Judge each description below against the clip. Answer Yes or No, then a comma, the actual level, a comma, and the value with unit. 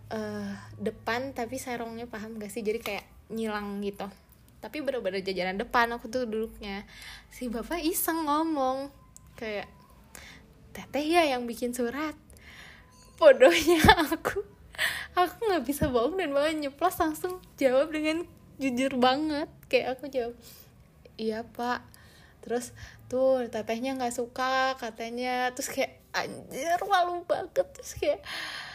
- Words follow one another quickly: No, average, 125 wpm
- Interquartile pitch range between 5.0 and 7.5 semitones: Yes, wide, 5.5 semitones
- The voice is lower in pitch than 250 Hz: No, very high, 255 Hz